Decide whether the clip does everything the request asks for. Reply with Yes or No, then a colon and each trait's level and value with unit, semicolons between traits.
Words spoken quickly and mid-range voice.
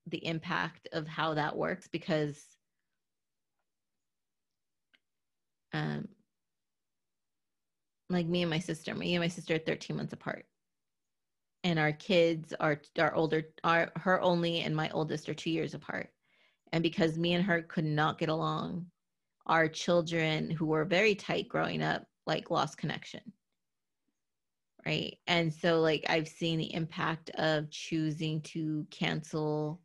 No: average, 140 wpm; medium, 160 Hz